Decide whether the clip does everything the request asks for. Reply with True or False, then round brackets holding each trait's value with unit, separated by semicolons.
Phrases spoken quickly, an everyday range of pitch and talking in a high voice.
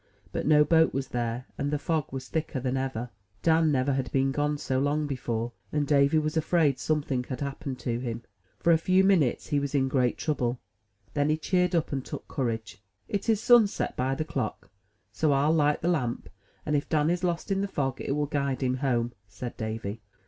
False (210 wpm; 3.5 semitones; 140 Hz)